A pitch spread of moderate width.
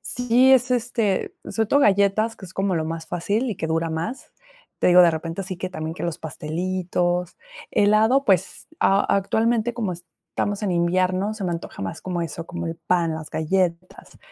Yes: average, 4.1 semitones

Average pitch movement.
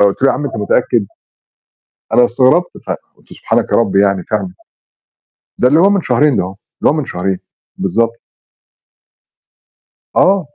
No: wide, 6.4 semitones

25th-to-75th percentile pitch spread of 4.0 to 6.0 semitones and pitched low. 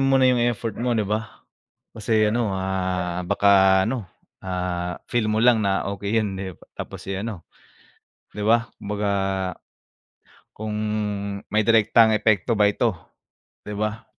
No: average, 2.8 semitones; low, 105 Hz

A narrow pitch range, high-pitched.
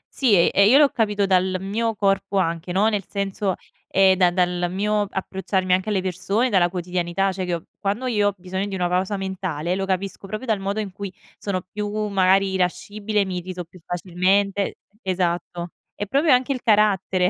Yes: narrow, 2.1 semitones; high, 195 Hz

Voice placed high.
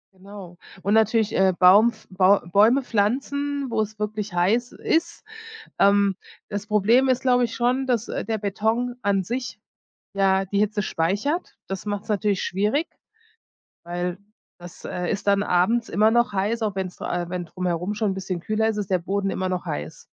Yes: high, 205 Hz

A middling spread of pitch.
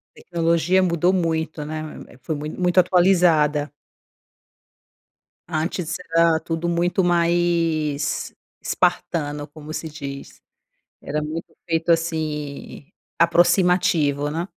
No: narrow, 2.3 semitones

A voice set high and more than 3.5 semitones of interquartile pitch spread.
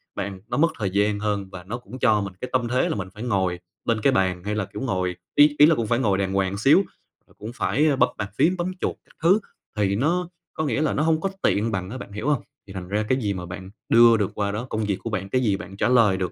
No: low, 105 Hz; average, 4.8 semitones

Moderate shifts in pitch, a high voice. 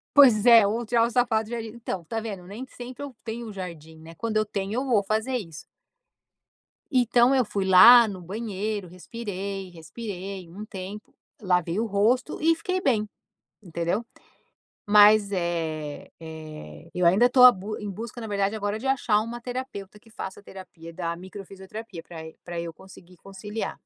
Yes: average, 4.1 semitones; high, 205 Hz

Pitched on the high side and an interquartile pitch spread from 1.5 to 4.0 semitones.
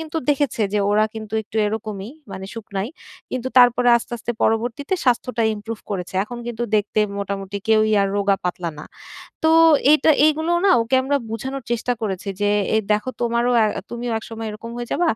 Yes: high, 225 Hz; average, 3.1 semitones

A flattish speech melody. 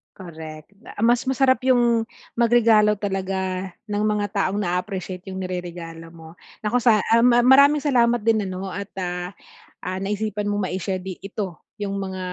No: average, 3.3 semitones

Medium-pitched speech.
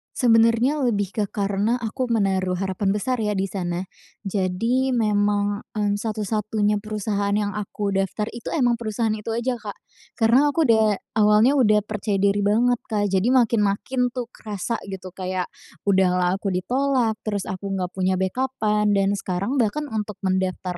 No: high, 210 Hz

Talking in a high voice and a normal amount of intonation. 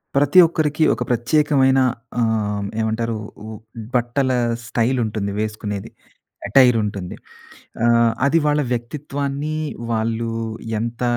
No: low, 120 Hz; average, 4.1 semitones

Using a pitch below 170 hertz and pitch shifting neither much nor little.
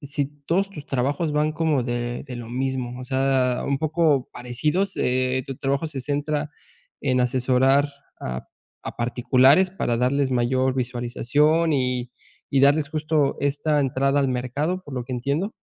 Yes: low, 135 Hz; average, 3.0 semitones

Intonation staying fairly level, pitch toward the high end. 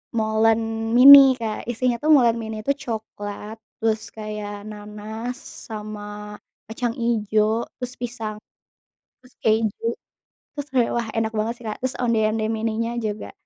Yes: narrow, 1.7 semitones; high, 225 Hz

